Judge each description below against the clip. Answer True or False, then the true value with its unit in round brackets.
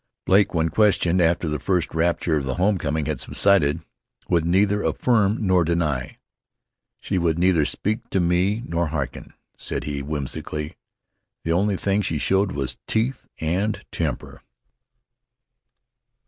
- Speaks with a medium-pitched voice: False (85 Hz)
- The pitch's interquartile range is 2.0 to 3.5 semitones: False (4.0 semitones)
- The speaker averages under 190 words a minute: True (140 wpm)